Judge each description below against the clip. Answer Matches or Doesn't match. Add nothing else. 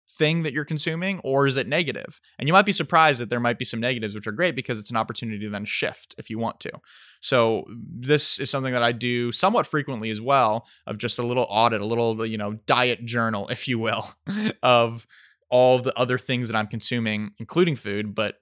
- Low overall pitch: Matches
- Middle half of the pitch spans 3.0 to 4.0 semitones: Matches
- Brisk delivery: Matches